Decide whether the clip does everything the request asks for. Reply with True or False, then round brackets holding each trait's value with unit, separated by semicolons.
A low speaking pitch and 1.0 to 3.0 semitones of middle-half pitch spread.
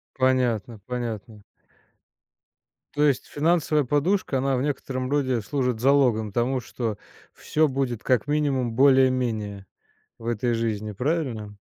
False (130 Hz; 3.5 semitones)